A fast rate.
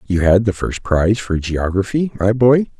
No: average, 195 wpm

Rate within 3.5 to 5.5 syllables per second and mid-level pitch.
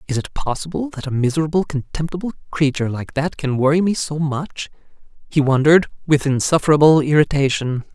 No: 5.9 syllables/s; medium, 150 Hz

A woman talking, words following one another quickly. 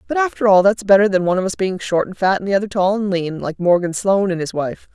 Yes: female; fast, 305 wpm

